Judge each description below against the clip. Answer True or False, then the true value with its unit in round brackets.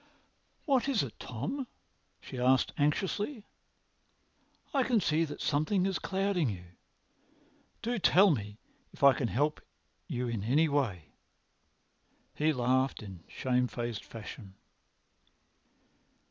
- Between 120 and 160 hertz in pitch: True (140 Hz)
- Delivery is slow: True (120 wpm)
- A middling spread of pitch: False (8.1 semitones)